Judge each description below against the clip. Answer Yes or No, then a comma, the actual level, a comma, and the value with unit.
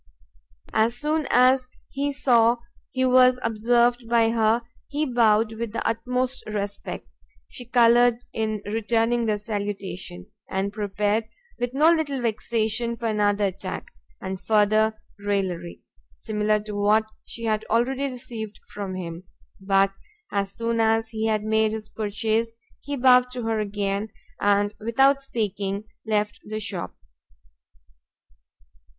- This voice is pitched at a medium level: No, high, 220 Hz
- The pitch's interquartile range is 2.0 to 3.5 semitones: Yes, average, 2.7 semitones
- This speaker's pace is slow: Yes, slow, 130 wpm